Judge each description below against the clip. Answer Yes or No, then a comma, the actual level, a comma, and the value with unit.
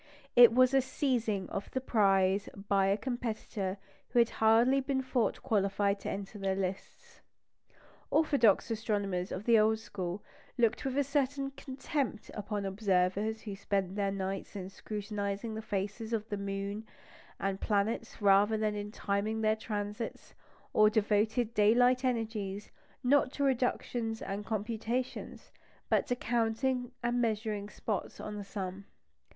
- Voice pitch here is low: No, high, 215 Hz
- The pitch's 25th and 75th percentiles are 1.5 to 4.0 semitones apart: Yes, average, 3.1 semitones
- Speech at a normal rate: Yes, average, 145 wpm